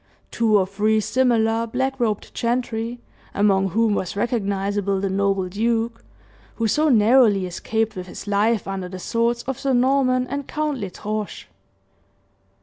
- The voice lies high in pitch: Yes, high, 220 Hz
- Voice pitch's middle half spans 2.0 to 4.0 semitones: Yes, average, 3.4 semitones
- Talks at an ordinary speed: Yes, average, 145 wpm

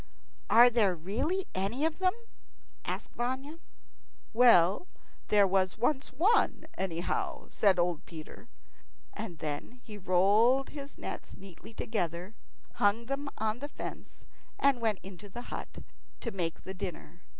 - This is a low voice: No, high, 215 Hz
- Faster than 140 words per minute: No, slow, 135 wpm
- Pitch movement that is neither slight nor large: No, wide, 5.9 semitones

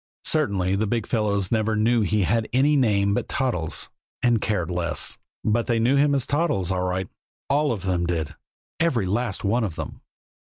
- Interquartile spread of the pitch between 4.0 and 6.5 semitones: Yes, average, 4.5 semitones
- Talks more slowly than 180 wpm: No, average, 185 wpm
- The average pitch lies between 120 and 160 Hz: No, low, 110 Hz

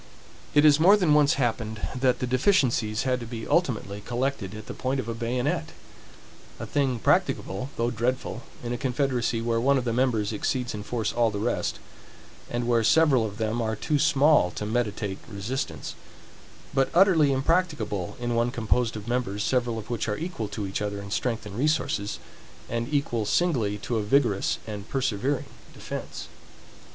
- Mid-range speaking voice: No, low, 120 Hz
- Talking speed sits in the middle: Yes, average, 175 wpm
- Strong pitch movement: No, average, 3.8 semitones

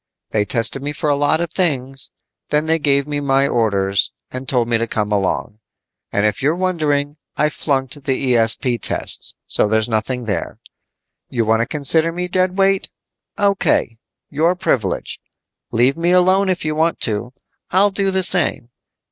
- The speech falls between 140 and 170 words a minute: Yes, average, 165 wpm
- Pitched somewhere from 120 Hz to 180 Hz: Yes, medium, 140 Hz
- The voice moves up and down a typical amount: No, wide, 6.4 semitones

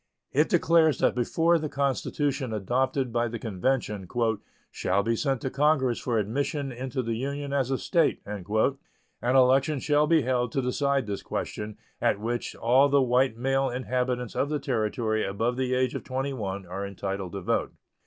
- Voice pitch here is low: Yes, low, 125 Hz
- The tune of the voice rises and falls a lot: No, average, 3.7 semitones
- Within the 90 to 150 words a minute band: No, average, 170 wpm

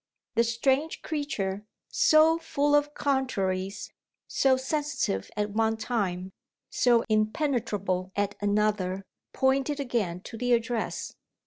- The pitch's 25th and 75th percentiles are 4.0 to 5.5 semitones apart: Yes, average, 5.2 semitones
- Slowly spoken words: Yes, slow, 110 wpm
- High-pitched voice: Yes, high, 230 Hz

